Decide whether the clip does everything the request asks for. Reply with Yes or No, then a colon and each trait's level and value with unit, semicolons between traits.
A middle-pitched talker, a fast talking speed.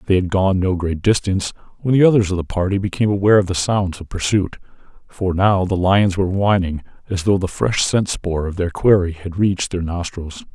No: very low, 95 Hz; fast, 215 wpm